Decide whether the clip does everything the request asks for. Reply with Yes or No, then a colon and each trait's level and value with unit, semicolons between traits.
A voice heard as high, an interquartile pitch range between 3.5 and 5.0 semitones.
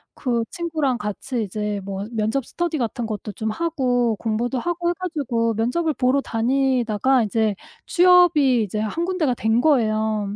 No: high, 245 Hz; wide, 5.5 semitones